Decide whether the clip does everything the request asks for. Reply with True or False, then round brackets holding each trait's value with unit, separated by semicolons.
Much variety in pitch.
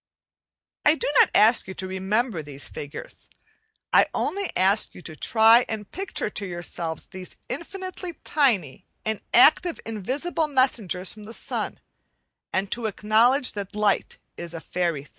True (5.8 semitones)